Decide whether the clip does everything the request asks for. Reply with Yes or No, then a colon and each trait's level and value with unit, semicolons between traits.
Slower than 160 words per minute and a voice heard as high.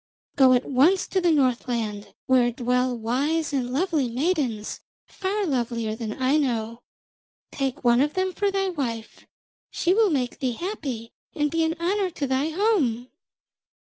Yes: average, 150 wpm; very high, 270 Hz